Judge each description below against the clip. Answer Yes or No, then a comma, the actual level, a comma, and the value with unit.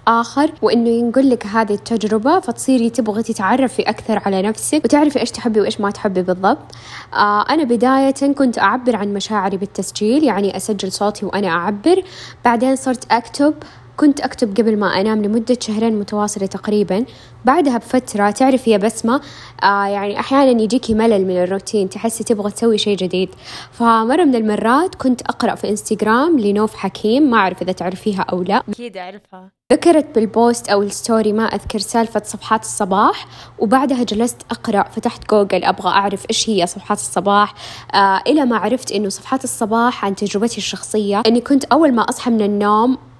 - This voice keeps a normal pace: No, fast, 160 wpm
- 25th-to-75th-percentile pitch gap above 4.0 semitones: No, average, 3.3 semitones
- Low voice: No, high, 220 Hz